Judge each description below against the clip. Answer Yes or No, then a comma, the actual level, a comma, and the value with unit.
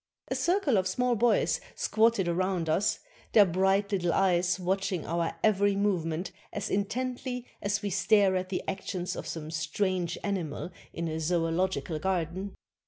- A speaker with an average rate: Yes, average, 150 wpm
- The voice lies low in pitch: No, high, 190 Hz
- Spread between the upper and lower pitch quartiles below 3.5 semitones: Yes, average, 2.9 semitones